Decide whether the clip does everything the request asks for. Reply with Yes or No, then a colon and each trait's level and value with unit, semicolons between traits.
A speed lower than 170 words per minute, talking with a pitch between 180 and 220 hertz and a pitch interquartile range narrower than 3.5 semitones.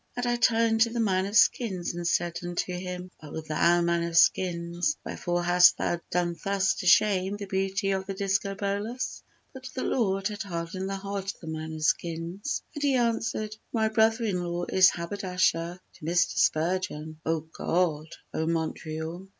No: average, 175 wpm; medium, 185 Hz; average, 3.1 semitones